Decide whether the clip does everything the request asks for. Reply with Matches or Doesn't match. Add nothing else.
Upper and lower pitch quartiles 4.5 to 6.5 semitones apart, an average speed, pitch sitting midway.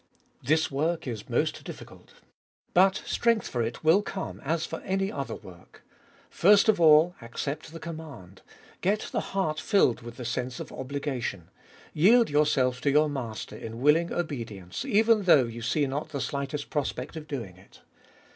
Matches